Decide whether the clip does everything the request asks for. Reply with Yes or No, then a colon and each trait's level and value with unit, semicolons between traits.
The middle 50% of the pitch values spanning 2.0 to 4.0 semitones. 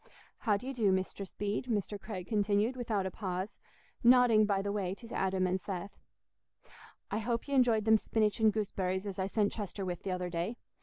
Yes: average, 2.8 semitones